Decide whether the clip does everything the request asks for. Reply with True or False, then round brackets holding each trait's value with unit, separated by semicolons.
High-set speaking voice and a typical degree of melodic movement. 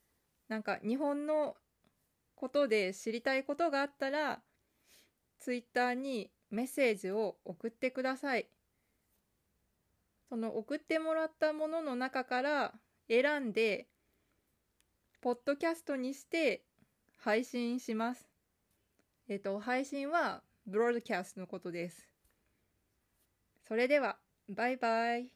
True (245 Hz; 4.3 semitones)